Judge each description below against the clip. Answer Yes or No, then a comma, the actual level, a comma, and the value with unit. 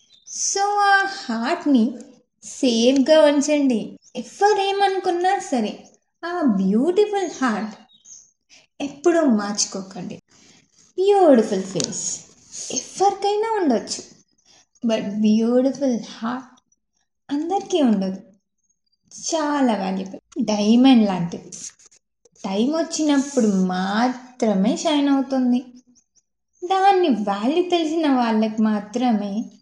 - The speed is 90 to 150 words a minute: No, slow, 70 wpm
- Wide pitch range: Yes, wide, 6.8 semitones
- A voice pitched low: No, very high, 250 Hz